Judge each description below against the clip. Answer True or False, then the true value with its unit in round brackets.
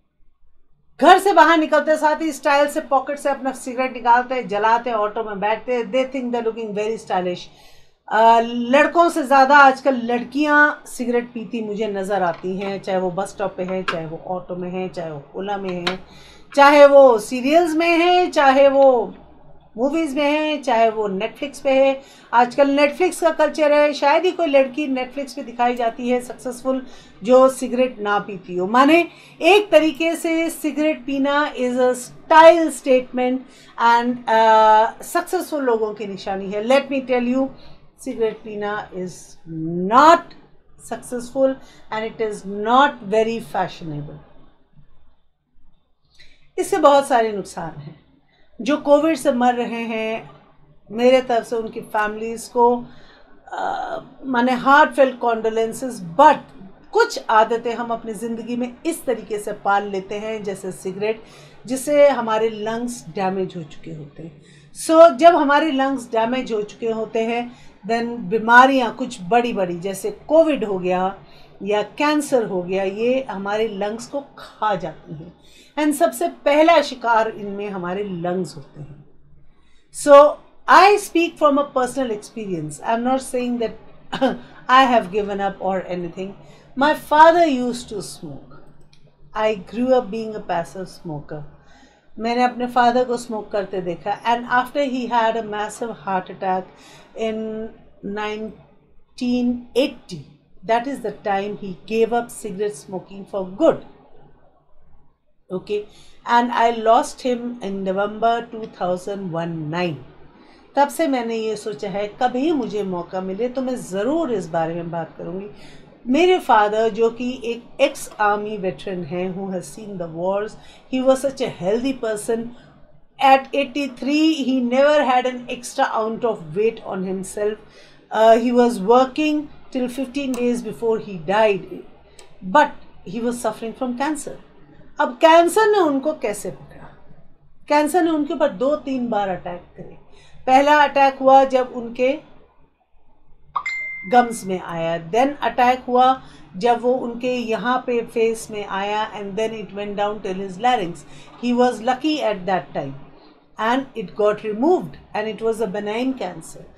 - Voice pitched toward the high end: True (230 Hz)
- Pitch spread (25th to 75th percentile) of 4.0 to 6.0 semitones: True (5.0 semitones)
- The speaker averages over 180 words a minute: False (140 wpm)